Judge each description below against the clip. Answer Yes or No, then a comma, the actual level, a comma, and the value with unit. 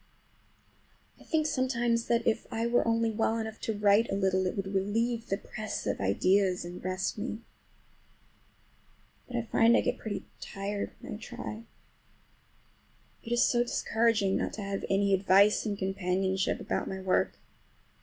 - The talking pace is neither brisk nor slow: Yes, average, 160 wpm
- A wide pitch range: No, average, 3.1 semitones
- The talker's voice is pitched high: Yes, high, 210 Hz